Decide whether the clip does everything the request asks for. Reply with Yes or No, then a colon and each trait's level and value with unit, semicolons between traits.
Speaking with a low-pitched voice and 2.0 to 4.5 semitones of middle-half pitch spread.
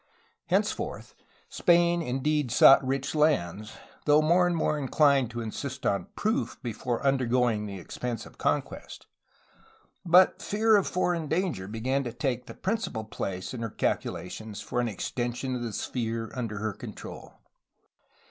No: low, 130 Hz; wide, 5.4 semitones